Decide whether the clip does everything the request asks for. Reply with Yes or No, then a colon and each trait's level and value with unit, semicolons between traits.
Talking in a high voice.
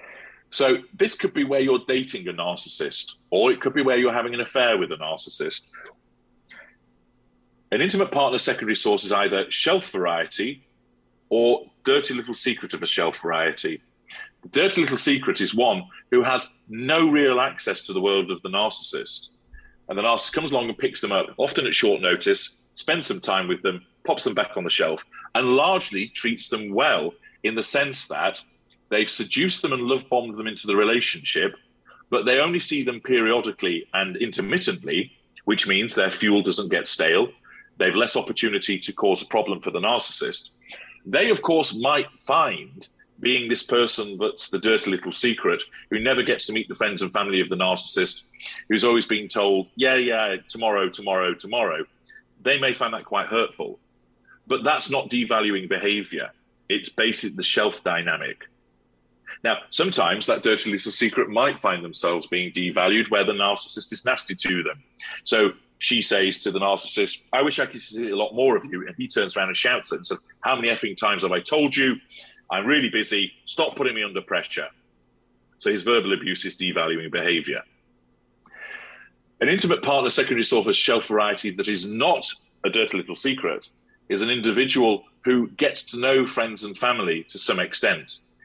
No: low, 125 Hz